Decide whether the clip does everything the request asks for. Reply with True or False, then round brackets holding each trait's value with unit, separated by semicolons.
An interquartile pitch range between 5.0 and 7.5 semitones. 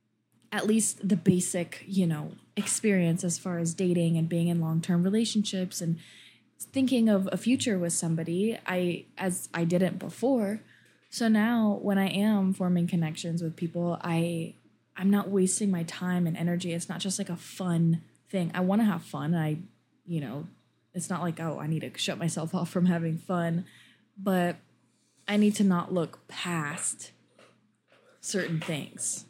False (2.6 semitones)